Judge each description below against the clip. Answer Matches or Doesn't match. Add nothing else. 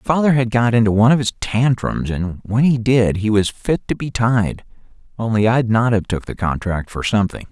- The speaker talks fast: Matches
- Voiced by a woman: Doesn't match